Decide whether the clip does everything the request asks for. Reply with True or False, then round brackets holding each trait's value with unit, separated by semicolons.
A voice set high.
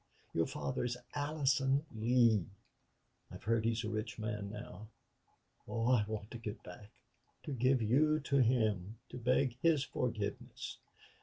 False (115 Hz)